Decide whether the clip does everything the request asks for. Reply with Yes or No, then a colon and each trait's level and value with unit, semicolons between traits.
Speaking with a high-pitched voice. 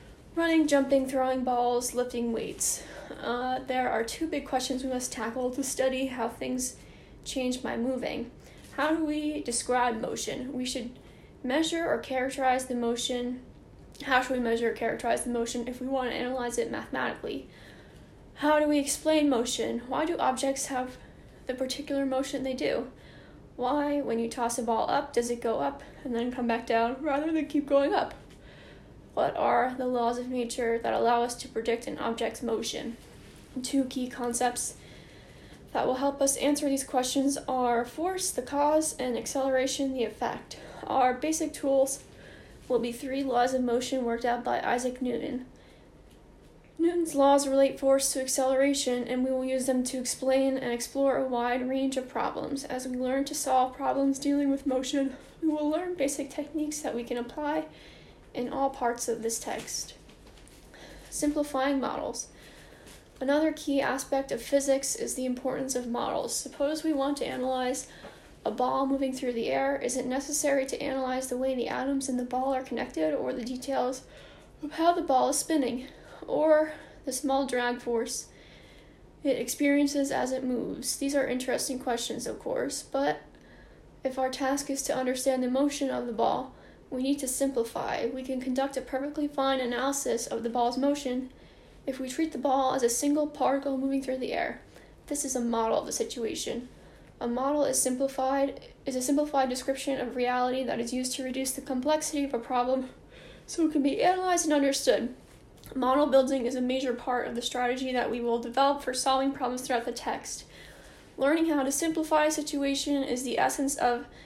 Yes: very high, 260 Hz